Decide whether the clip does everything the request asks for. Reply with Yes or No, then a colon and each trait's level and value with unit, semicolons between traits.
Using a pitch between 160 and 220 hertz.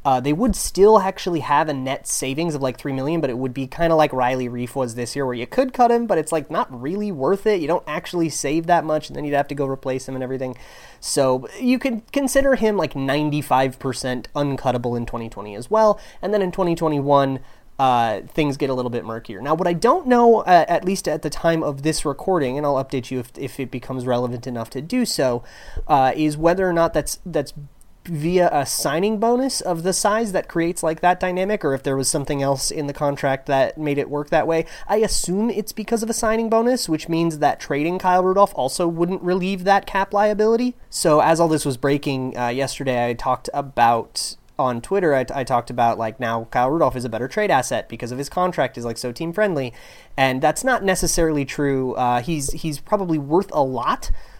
No: medium, 150 Hz